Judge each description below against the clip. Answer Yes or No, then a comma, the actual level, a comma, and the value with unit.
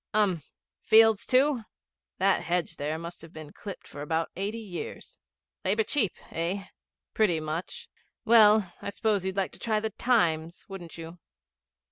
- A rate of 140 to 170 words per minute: Yes, average, 150 wpm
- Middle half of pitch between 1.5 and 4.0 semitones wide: No, average, 4.5 semitones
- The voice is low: No, high, 190 Hz